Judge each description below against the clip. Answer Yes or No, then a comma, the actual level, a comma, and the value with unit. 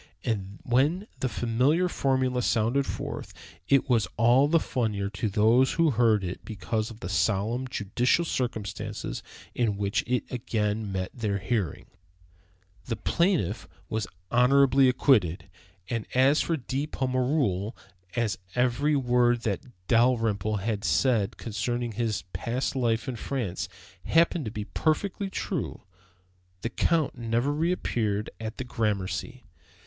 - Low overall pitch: Yes, low, 120 Hz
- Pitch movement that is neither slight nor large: Yes, average, 3.7 semitones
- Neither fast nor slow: No, slow, 130 wpm